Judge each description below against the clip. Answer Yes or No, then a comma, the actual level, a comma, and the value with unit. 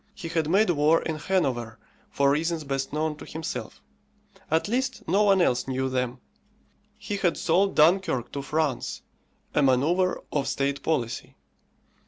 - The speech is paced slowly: No, average, 150 wpm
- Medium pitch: Yes, medium, 155 Hz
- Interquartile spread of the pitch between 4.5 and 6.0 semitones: Yes, average, 4.8 semitones